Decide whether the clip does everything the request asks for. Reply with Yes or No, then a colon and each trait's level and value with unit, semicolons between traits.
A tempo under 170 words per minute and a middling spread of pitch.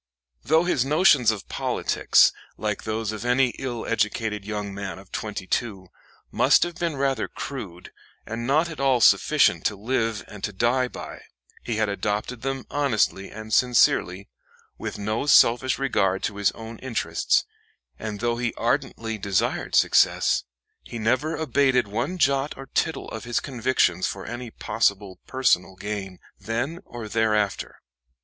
Yes: average, 150 wpm; average, 4.1 semitones